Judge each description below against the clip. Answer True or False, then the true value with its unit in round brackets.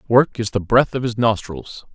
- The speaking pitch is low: True (115 Hz)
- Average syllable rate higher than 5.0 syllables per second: False (4.6 syllables/s)